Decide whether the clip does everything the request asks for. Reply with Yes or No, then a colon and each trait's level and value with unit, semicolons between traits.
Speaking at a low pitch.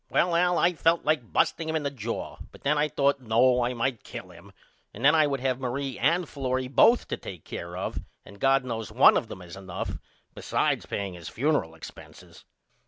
Yes: low, 130 Hz